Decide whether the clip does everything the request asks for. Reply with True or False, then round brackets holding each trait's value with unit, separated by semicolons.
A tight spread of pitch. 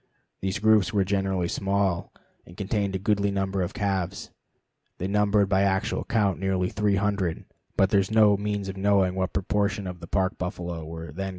True (1.4 semitones)